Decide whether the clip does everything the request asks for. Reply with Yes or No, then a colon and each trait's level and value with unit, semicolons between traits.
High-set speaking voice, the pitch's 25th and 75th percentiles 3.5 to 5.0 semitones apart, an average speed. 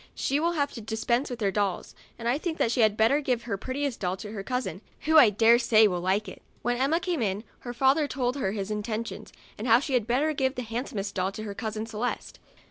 No: high, 235 Hz; average, 3.9 semitones; fast, 245 wpm